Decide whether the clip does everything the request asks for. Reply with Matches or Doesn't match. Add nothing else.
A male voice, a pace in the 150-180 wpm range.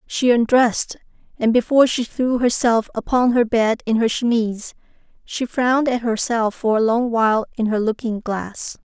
Doesn't match